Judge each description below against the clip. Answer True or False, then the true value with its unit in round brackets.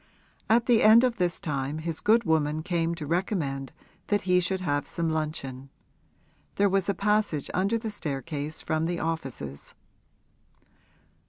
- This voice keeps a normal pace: True (150 wpm)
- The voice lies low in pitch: False (165 Hz)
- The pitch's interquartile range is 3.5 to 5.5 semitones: True (4.9 semitones)